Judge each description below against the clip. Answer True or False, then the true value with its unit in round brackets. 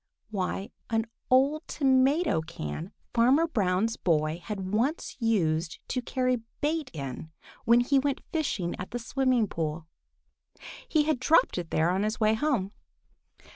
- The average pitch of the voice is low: False (225 Hz)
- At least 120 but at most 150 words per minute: True (140 wpm)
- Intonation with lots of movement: True (6.9 semitones)